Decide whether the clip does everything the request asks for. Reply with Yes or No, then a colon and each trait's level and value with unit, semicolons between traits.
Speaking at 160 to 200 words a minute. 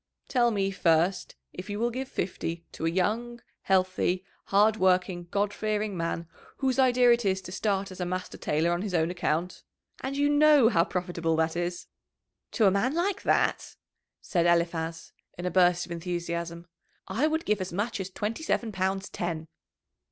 Yes: average, 180 wpm